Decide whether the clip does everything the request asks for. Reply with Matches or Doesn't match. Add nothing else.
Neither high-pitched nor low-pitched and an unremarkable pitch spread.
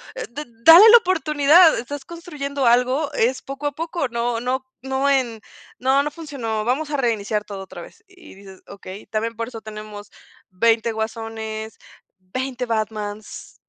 Doesn't match